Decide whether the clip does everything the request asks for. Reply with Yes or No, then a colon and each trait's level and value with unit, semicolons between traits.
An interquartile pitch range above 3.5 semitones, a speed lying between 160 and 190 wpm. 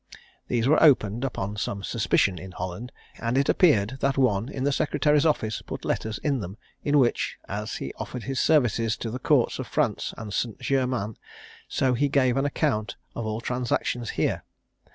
Yes: average, 4.1 semitones; average, 180 wpm